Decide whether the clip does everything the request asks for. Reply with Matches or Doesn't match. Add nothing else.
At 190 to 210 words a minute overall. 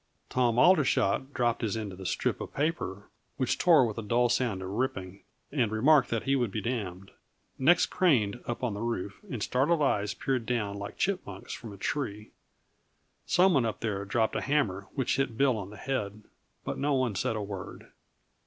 Matches